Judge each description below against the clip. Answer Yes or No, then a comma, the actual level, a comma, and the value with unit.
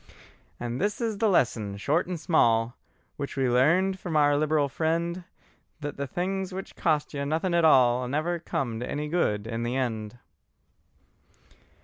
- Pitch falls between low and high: Yes, medium, 150 Hz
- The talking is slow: No, average, 160 wpm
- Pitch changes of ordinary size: No, wide, 5.7 semitones